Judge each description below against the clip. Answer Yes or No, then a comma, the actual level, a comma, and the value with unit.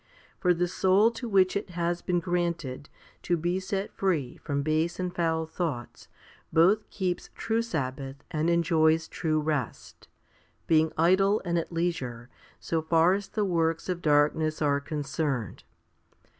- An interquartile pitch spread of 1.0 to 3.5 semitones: Yes, average, 2.7 semitones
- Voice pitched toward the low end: No, medium, 165 Hz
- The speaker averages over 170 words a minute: No, average, 145 wpm